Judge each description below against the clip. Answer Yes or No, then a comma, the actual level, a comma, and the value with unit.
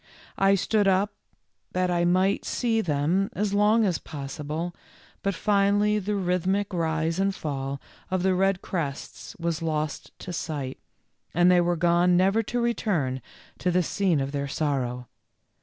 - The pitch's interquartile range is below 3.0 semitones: No, average, 4.1 semitones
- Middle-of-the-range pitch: Yes, medium, 180 Hz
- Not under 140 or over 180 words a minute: Yes, average, 155 wpm